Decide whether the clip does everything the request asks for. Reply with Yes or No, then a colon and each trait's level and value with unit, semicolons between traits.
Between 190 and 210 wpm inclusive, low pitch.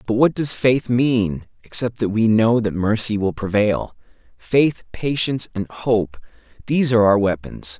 No: average, 155 wpm; low, 110 Hz